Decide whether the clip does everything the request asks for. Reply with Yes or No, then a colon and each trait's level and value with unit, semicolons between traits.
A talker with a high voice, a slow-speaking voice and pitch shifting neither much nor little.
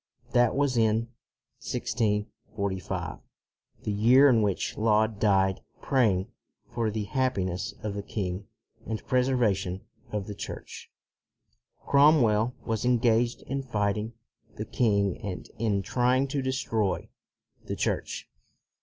No: low, 110 Hz; slow, 125 wpm; average, 3.5 semitones